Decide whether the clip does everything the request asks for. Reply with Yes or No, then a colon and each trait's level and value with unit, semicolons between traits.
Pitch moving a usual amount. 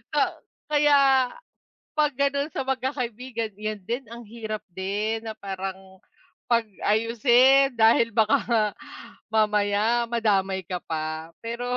Yes: average, 3.0 semitones